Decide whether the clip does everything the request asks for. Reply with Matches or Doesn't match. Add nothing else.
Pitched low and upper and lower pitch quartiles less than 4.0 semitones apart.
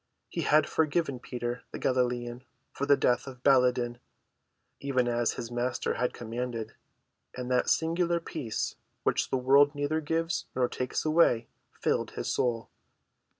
Matches